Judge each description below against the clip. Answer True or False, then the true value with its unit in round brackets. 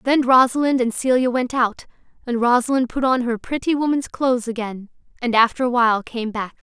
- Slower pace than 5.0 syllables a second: False (5.5 syllables/s)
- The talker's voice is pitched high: True (245 Hz)